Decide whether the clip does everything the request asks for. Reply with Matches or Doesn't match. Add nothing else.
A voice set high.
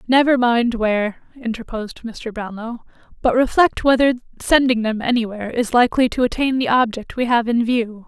Matches